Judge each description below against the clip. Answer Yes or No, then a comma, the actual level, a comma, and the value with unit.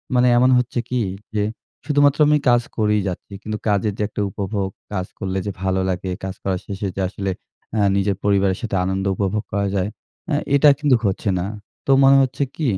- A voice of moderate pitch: No, low, 105 Hz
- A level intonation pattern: No, average, 4.4 semitones